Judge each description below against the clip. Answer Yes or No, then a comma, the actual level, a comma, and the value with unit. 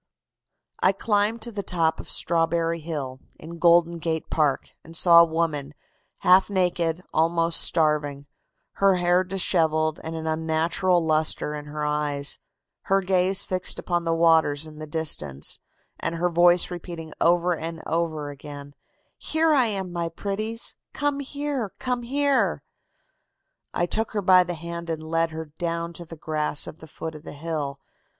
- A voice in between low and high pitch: Yes, medium, 165 Hz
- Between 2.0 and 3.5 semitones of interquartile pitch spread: Yes, narrow, 2.5 semitones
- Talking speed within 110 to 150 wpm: No, average, 160 wpm